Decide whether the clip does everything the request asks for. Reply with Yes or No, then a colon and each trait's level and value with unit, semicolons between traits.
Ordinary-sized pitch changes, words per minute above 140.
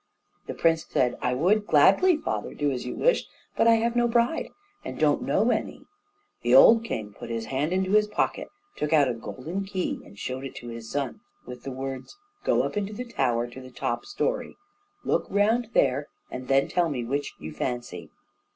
No: wide, 8.8 semitones; average, 200 wpm